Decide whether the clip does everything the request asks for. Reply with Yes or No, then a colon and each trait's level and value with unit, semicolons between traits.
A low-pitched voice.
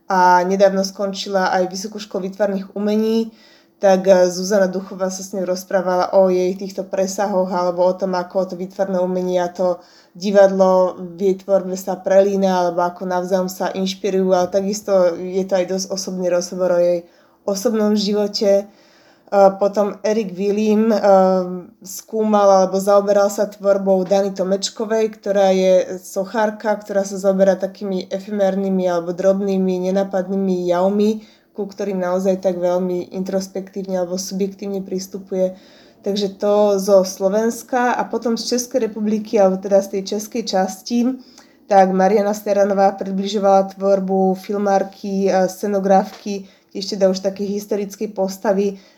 No: high, 195 Hz